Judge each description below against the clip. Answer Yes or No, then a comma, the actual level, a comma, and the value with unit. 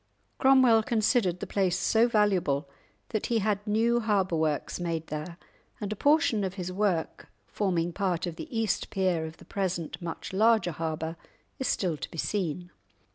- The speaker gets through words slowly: No, average, 170 wpm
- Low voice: No, high, 190 Hz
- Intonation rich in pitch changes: No, average, 4.3 semitones